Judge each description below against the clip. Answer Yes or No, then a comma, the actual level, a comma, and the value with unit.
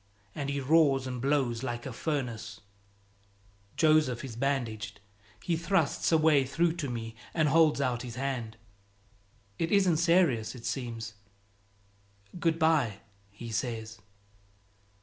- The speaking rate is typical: No, slow, 130 wpm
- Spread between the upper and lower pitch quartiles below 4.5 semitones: No, average, 5.1 semitones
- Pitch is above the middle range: No, low, 135 Hz